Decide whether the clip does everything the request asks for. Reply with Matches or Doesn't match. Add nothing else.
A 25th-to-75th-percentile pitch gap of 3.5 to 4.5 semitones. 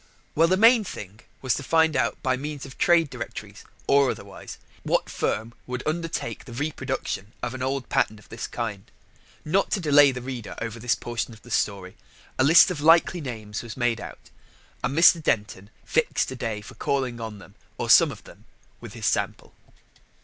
Doesn't match